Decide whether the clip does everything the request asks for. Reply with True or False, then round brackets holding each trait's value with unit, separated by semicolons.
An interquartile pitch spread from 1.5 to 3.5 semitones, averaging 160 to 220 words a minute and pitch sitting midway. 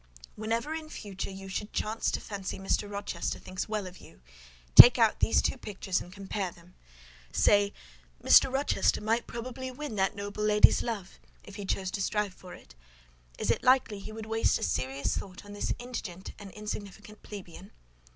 False (2.6 semitones; 180 wpm; 205 Hz)